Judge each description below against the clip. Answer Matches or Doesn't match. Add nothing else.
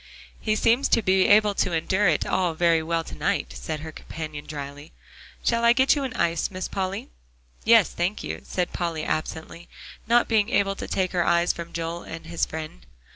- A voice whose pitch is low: Doesn't match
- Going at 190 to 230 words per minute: Matches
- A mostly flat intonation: Doesn't match